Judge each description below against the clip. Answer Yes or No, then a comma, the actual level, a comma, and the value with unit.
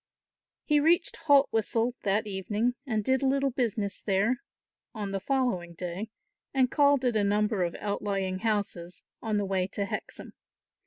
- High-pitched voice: Yes, high, 215 Hz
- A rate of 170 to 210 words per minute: No, average, 155 wpm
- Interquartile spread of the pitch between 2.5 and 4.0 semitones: No, average, 4.6 semitones